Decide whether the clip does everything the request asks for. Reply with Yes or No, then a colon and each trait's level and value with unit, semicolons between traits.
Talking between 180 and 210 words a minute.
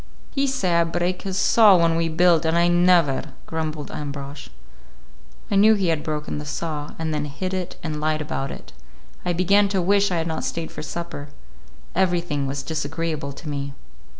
Yes: average, 185 wpm